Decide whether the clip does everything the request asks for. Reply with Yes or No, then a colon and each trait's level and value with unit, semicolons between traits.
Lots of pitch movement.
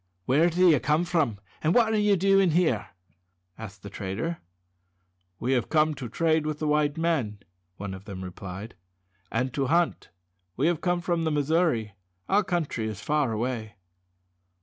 Yes: wide, 7.3 semitones